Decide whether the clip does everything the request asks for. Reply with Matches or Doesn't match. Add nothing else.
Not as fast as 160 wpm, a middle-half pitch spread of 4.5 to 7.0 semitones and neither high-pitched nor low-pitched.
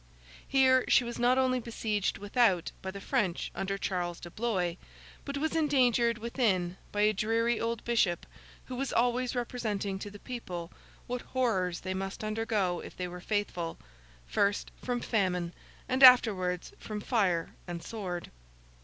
Doesn't match